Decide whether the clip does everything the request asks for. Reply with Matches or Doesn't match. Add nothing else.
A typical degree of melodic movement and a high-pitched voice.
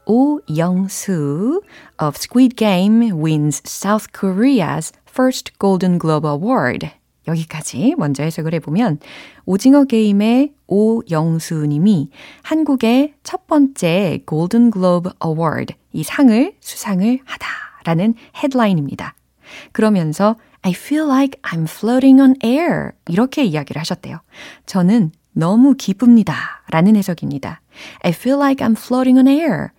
Doesn't match